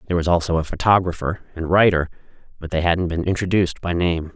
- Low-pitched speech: Yes, very low, 85 Hz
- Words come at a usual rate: Yes, average, 195 wpm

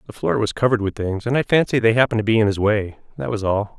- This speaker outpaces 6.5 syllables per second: Yes, 7.0 syllables/s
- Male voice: Yes, male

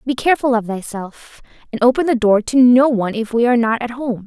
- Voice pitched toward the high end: Yes, high, 240 Hz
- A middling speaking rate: No, fast, 240 wpm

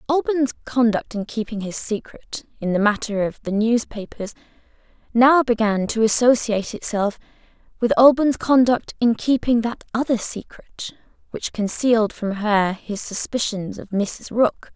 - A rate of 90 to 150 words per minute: Yes, average, 140 wpm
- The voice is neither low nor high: No, high, 225 Hz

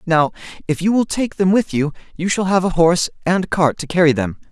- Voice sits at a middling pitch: Yes, medium, 170 Hz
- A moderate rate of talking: No, fast, 240 wpm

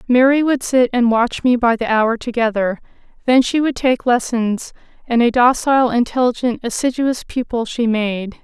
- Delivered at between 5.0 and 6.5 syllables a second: No, 4.8 syllables/s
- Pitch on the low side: No, high, 240 Hz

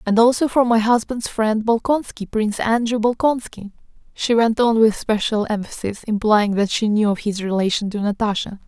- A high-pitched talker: Yes, high, 220 Hz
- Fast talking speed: No, average, 175 wpm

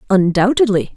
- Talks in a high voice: Yes, high, 205 Hz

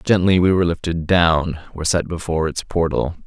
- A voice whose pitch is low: Yes, very low, 85 Hz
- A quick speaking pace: No, average, 185 wpm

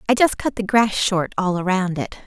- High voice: Yes, high, 200 Hz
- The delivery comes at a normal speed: No, fast, 240 wpm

